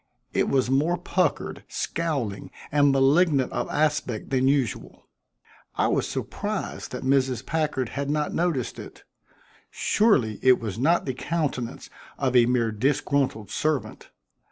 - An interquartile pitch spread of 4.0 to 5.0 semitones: No, average, 3.3 semitones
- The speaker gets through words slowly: Yes, slow, 130 wpm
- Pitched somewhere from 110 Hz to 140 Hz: Yes, low, 135 Hz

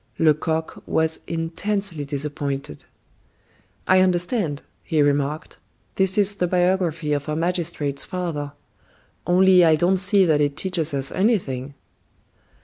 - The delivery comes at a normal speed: No, slow, 120 wpm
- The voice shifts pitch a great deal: No, average, 4.0 semitones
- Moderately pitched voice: Yes, medium, 165 Hz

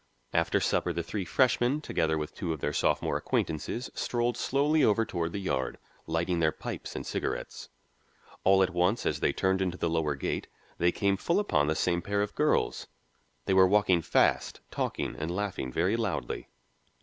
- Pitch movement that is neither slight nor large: Yes, average, 4.1 semitones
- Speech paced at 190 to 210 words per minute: No, average, 180 wpm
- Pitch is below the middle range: Yes, very low, 90 Hz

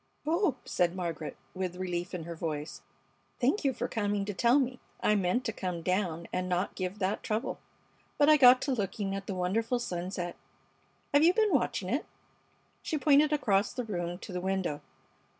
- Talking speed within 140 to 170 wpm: No, average, 185 wpm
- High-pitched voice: Yes, high, 195 Hz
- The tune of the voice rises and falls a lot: Yes, wide, 5.7 semitones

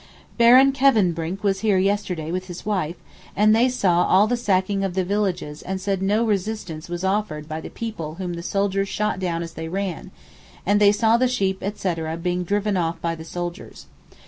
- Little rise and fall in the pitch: No, average, 3.3 semitones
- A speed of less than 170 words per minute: No, average, 195 wpm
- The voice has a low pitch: No, high, 190 Hz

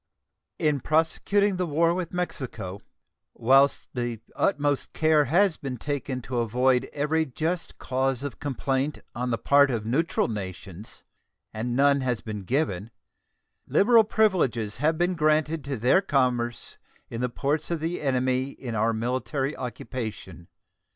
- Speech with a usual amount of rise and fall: Yes, average, 4.6 semitones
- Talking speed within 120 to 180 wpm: Yes, average, 140 wpm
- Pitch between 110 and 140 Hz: Yes, low, 135 Hz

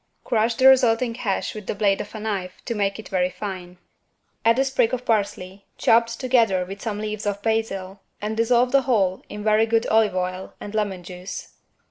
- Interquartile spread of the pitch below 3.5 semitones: Yes, average, 2.9 semitones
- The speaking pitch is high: Yes, high, 215 Hz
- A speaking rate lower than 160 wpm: No, average, 195 wpm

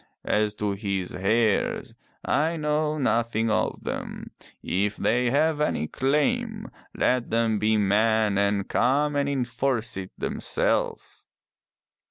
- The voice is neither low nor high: No, low, 115 Hz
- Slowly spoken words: Yes, slow, 125 wpm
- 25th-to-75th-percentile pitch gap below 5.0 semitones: No, wide, 5.5 semitones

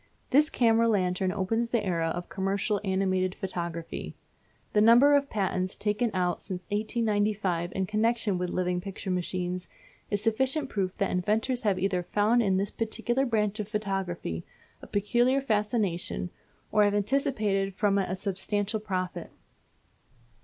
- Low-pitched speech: No, high, 205 Hz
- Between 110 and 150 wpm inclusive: Yes, average, 145 wpm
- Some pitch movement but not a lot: Yes, average, 3.2 semitones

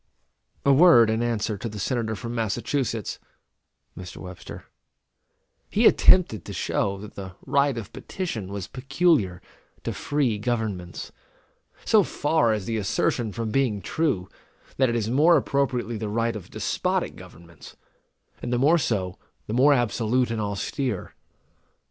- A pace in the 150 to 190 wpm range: No, average, 140 wpm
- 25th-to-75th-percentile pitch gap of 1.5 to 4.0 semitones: No, average, 4.6 semitones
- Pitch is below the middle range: Yes, low, 115 Hz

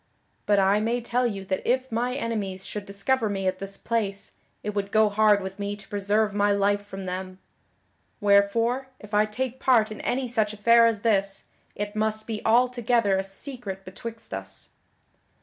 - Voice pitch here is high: Yes, high, 210 Hz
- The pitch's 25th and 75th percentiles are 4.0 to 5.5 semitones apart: No, average, 2.7 semitones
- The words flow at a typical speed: Yes, average, 180 wpm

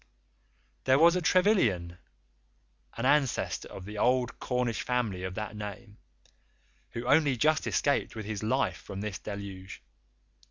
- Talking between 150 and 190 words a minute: No, slow, 135 wpm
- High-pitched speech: No, low, 115 Hz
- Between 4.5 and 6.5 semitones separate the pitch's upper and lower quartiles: Yes, average, 5.0 semitones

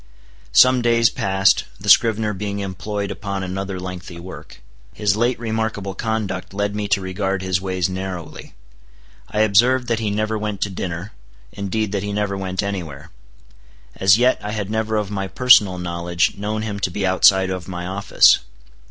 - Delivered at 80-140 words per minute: No, average, 170 wpm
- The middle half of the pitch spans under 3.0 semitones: Yes, narrow, 2.4 semitones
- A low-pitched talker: Yes, low, 100 Hz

